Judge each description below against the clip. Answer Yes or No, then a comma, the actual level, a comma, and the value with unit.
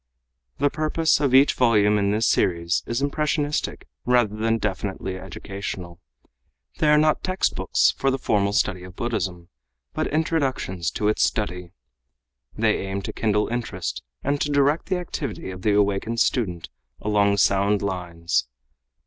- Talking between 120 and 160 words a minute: Yes, average, 145 wpm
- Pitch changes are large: Yes, wide, 6.2 semitones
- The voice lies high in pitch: No, low, 105 Hz